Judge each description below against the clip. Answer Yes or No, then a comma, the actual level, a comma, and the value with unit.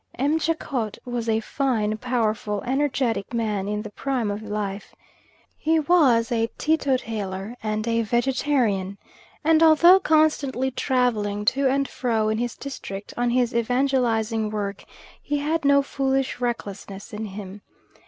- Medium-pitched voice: No, high, 240 Hz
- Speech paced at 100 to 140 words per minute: Yes, slow, 135 wpm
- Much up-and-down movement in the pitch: No, average, 4.4 semitones